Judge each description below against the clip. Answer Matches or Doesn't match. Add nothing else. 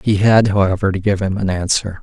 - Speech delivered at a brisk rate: Matches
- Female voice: Doesn't match